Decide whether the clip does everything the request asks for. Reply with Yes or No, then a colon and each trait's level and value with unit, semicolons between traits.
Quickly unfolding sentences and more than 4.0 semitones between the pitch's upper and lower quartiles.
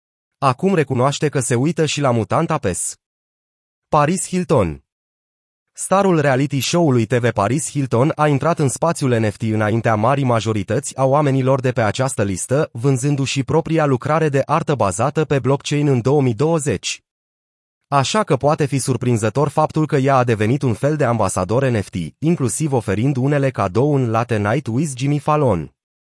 No: average, 150 wpm; average, 4.4 semitones